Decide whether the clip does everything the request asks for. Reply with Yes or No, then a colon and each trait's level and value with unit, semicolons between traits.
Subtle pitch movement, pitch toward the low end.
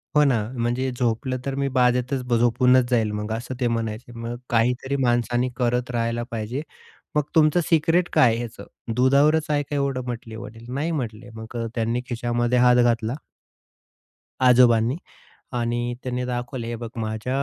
Yes: narrow, 1.9 semitones; low, 120 Hz